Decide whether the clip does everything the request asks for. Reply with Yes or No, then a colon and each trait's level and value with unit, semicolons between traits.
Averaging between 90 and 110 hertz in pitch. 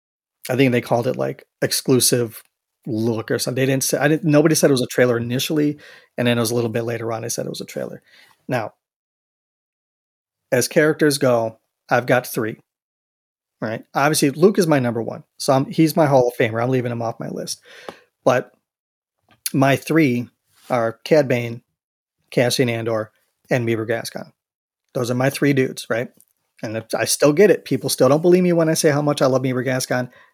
No: low, 130 Hz